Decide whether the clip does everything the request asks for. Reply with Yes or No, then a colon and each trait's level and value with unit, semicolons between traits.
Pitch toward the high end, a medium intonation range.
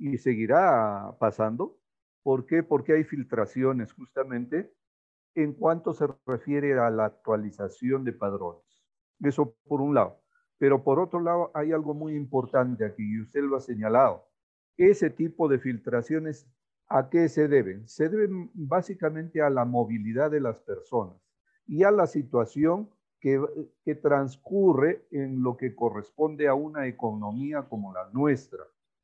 No: medium, 140 Hz; average, 4.4 semitones